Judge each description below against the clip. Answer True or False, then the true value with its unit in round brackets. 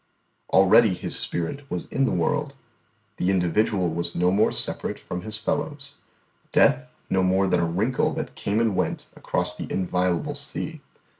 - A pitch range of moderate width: False (6.4 semitones)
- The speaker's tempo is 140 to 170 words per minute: True (160 wpm)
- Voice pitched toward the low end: True (95 Hz)